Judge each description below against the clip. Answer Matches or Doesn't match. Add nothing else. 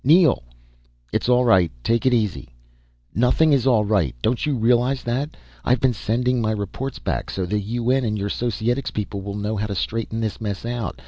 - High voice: Doesn't match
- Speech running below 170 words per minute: Doesn't match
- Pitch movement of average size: Matches